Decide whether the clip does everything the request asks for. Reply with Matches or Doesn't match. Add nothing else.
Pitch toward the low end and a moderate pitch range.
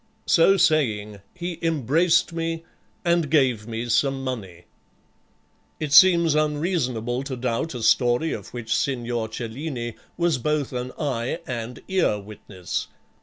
Doesn't match